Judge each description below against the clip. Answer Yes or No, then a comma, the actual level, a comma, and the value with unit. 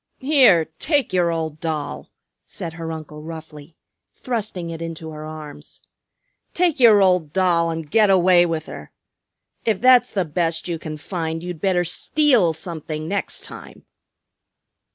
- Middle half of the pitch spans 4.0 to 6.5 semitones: No, average, 3.2 semitones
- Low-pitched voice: No, medium, 170 Hz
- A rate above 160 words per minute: No, average, 145 wpm